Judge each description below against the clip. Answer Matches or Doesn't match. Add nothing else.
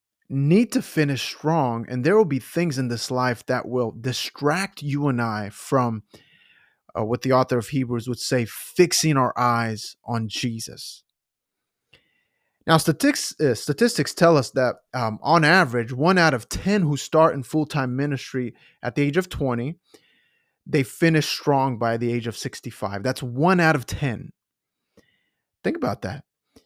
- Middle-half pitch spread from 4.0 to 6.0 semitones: Matches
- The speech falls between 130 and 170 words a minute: Matches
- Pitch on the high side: Doesn't match